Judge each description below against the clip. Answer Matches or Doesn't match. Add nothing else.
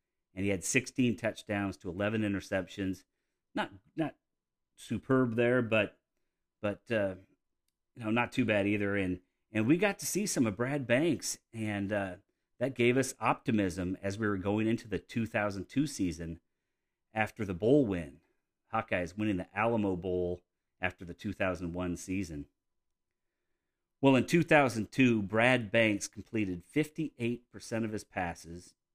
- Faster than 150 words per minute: Doesn't match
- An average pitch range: Matches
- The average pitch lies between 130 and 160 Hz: Doesn't match